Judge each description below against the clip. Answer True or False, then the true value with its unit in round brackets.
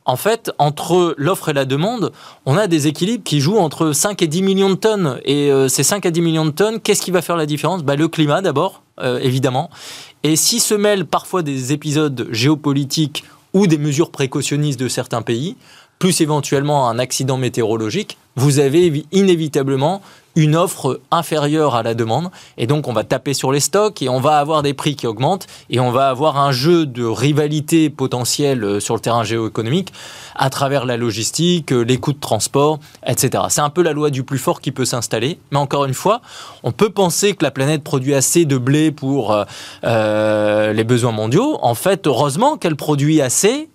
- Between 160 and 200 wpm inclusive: True (195 wpm)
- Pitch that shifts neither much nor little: True (4.3 semitones)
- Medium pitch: True (145 Hz)